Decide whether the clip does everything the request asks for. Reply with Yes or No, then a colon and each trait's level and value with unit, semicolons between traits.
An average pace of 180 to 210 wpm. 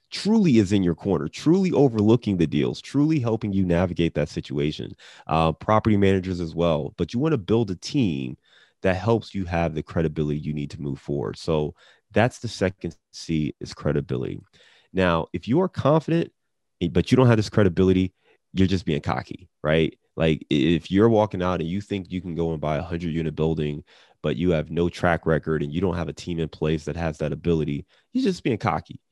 Yes: fast, 205 wpm